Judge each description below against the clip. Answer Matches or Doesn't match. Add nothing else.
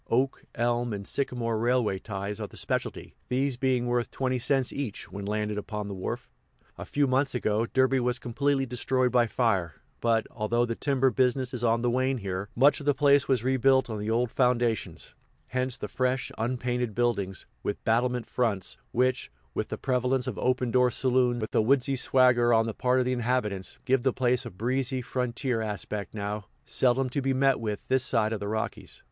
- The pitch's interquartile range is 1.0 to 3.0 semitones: Matches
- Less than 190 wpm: Doesn't match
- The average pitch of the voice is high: Doesn't match